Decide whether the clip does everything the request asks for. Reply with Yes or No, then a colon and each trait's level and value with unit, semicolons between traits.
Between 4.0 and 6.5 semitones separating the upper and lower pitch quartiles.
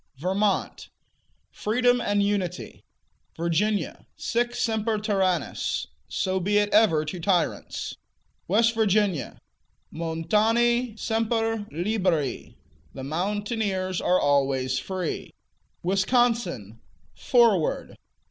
Yes: average, 4.6 semitones